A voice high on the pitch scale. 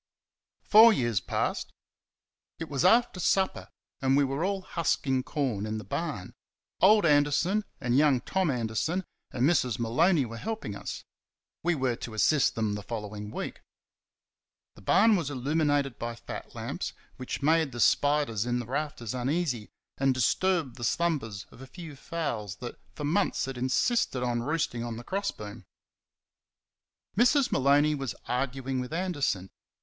No: low, 135 Hz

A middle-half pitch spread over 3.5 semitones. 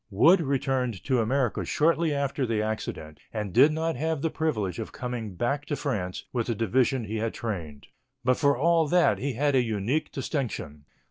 Yes: average, 5.0 semitones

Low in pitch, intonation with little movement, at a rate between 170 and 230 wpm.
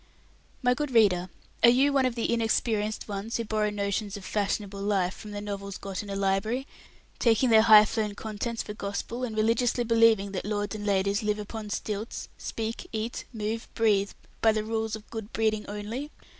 No: high, 215 Hz; narrow, 2.0 semitones; average, 185 wpm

